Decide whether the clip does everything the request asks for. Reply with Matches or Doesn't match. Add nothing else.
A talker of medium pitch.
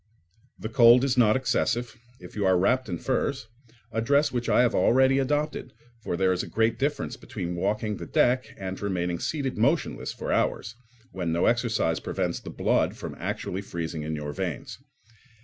Doesn't match